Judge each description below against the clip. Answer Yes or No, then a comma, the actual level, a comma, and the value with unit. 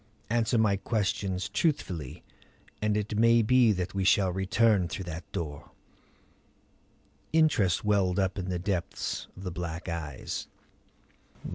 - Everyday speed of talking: No, slow, 130 wpm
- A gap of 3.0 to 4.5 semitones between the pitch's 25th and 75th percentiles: Yes, average, 3.3 semitones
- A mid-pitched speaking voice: No, very low, 95 Hz